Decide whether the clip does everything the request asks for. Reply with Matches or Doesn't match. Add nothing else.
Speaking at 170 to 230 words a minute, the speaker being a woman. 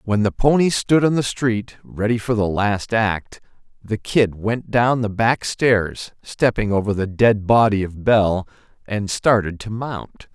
Doesn't match